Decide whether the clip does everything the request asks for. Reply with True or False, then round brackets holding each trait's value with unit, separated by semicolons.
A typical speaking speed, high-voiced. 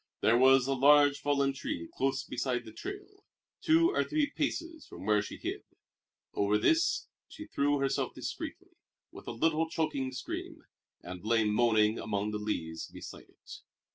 False (160 wpm; 135 Hz)